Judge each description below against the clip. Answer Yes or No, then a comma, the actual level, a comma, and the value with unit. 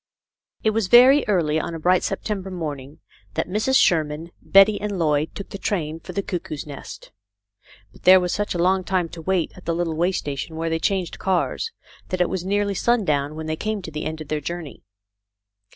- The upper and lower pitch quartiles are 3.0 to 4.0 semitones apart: Yes, average, 3.7 semitones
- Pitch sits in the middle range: Yes, medium, 175 Hz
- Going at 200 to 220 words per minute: Yes, fast, 205 wpm